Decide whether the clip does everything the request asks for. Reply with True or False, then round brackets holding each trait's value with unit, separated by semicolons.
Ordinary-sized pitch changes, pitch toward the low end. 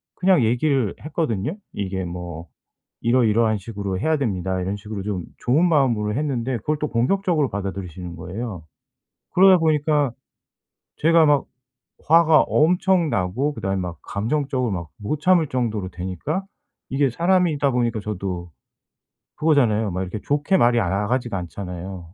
False (7.6 semitones; 115 Hz)